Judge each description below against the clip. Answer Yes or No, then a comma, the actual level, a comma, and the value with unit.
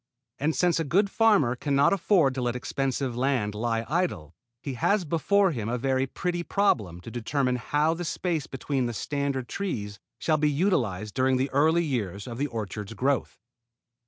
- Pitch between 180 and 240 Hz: No, low, 135 Hz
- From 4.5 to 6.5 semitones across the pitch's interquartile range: Yes, wide, 5.4 semitones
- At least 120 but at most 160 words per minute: No, average, 180 wpm